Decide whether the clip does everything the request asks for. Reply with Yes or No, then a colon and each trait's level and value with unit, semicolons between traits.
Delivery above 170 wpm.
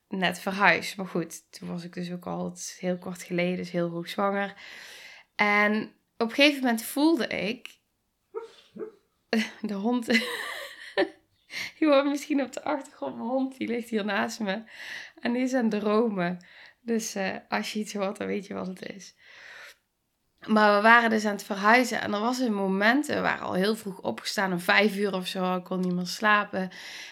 Yes: average, 190 wpm